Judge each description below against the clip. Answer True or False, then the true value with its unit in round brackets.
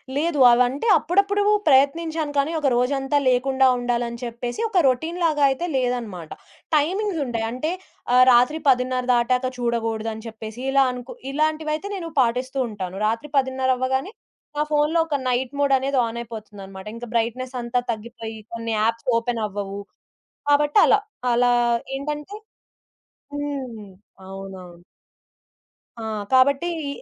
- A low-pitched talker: False (255 Hz)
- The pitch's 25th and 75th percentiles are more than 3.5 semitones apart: True (3.9 semitones)